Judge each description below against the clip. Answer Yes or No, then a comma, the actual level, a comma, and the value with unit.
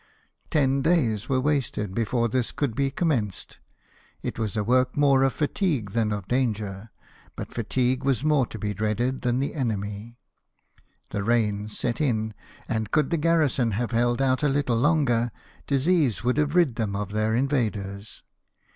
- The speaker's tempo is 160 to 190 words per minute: Yes, average, 165 wpm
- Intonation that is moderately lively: Yes, average, 4.2 semitones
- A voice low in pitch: Yes, low, 120 Hz